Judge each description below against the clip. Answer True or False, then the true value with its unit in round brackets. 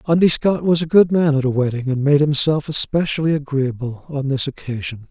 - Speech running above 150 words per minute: True (200 wpm)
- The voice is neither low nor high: True (145 Hz)